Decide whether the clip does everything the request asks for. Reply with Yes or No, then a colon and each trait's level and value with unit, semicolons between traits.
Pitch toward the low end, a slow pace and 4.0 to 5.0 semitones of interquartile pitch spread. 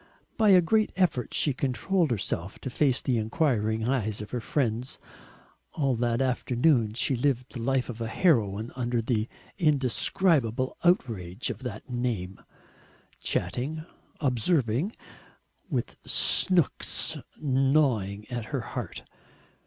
Yes: low, 125 Hz; slow, 120 wpm; average, 4.5 semitones